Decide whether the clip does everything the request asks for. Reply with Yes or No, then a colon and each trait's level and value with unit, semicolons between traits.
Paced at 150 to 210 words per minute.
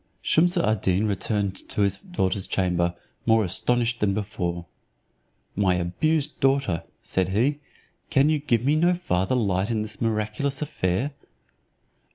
No: average, 140 wpm